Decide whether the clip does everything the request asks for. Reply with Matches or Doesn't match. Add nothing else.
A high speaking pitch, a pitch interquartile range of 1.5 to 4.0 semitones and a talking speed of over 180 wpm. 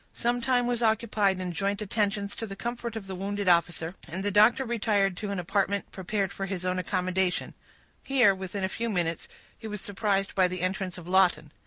Matches